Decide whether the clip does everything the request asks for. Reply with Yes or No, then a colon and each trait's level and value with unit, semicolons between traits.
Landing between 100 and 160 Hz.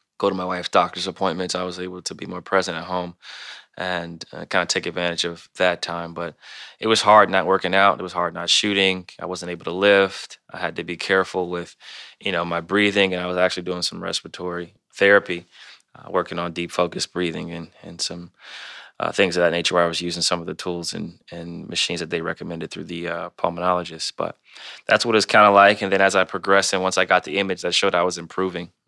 No: very low, 90 Hz